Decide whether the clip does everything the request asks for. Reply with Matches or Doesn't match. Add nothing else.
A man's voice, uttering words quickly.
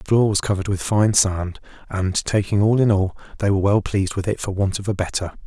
Matches